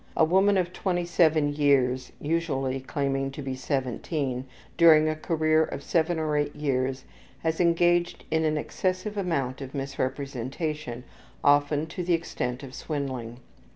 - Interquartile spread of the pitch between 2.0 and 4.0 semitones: Yes, average, 3.6 semitones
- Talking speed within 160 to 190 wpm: No, average, 140 wpm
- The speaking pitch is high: No, medium, 150 Hz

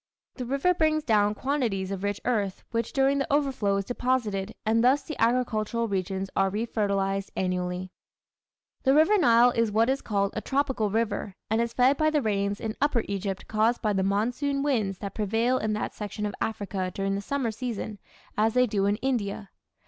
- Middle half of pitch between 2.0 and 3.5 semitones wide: No, average, 4.1 semitones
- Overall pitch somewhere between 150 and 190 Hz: No, high, 220 Hz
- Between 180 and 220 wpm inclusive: Yes, average, 185 wpm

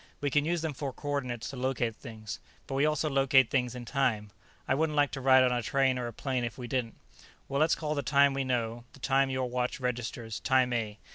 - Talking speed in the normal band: No, fast, 235 wpm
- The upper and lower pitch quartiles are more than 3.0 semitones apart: No, narrow, 2.4 semitones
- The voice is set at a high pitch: No, low, 130 Hz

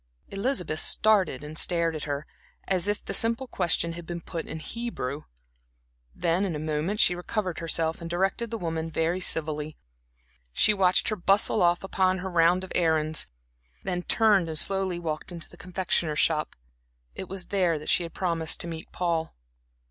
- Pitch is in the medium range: Yes, medium, 175 Hz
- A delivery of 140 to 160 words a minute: No, average, 175 wpm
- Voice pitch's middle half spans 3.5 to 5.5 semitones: No, average, 2.8 semitones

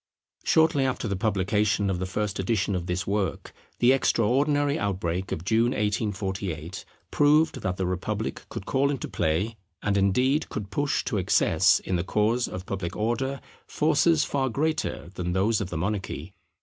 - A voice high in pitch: No, low, 105 Hz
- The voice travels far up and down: Yes, wide, 5.7 semitones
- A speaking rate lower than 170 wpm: Yes, average, 160 wpm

